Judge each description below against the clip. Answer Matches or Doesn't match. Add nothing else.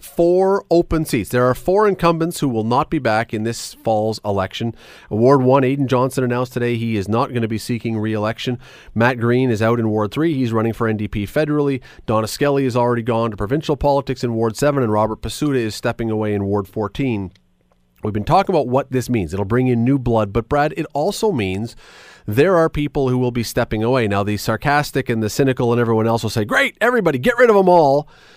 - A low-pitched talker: Matches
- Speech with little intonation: Doesn't match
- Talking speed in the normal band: Doesn't match